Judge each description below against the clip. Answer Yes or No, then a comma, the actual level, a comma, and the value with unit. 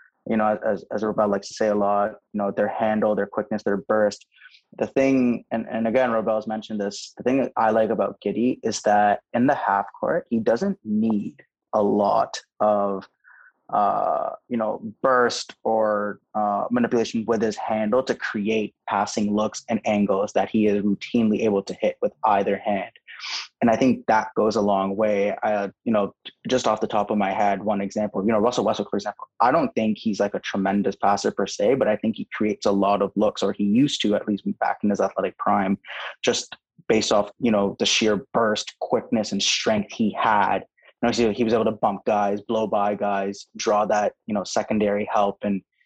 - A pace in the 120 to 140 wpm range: No, fast, 205 wpm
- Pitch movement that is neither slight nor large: No, narrow, 1.6 semitones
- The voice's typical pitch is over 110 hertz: No, low, 105 Hz